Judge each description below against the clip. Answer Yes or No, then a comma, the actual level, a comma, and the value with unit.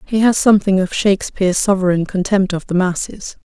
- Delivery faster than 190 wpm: No, average, 175 wpm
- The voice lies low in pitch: No, high, 190 Hz